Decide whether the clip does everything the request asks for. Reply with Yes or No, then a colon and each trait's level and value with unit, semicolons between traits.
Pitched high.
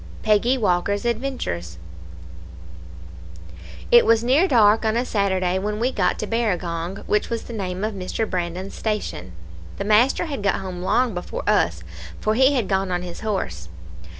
Yes: high, 205 Hz